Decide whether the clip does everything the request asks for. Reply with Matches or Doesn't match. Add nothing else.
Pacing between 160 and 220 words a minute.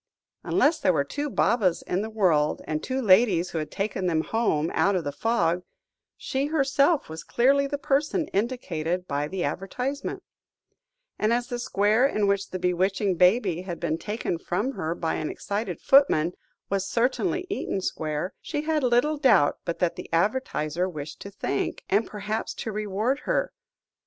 Matches